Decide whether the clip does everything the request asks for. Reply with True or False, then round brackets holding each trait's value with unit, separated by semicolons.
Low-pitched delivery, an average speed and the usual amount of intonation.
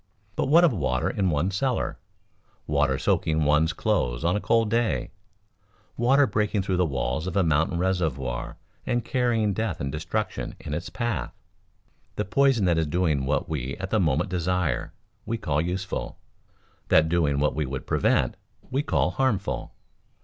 False (90 Hz; 165 wpm; 6.4 semitones)